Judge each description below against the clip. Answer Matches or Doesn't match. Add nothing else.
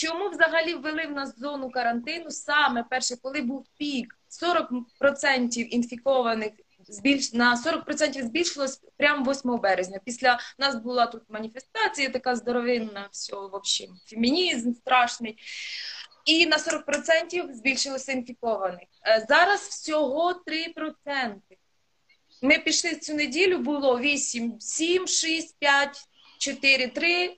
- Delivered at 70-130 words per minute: Matches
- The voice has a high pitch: Matches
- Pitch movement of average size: Matches